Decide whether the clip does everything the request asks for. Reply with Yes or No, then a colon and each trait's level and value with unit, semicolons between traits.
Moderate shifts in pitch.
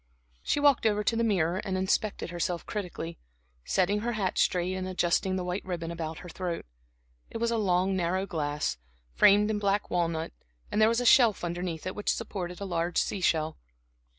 Yes: average, 3.2 semitones